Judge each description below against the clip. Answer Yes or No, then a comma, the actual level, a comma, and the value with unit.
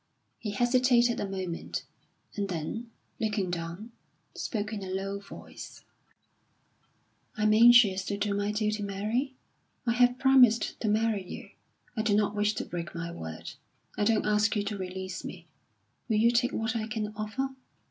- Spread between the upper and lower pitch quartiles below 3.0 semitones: Yes, narrow, 2.6 semitones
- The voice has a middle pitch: No, high, 210 Hz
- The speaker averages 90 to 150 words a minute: No, average, 165 wpm